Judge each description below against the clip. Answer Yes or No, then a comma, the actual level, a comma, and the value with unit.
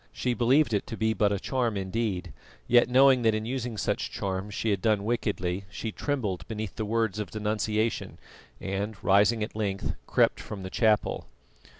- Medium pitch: No, low, 110 Hz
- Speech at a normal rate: Yes, average, 180 wpm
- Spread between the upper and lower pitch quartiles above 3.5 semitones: No, narrow, 2.6 semitones